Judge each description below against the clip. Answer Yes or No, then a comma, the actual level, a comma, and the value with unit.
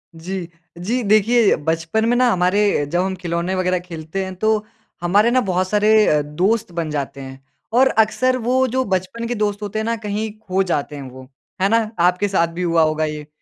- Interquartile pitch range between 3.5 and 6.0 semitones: Yes, average, 4.4 semitones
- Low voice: No, high, 190 Hz